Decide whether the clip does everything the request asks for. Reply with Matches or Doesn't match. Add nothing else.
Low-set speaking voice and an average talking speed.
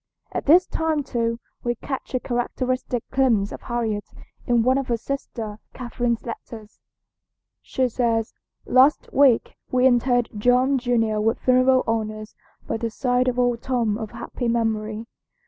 Doesn't match